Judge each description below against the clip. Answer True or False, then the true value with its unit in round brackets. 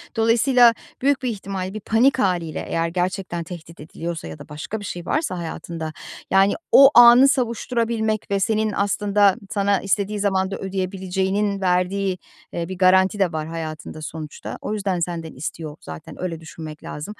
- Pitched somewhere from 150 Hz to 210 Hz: True (190 Hz)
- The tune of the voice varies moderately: True (3.9 semitones)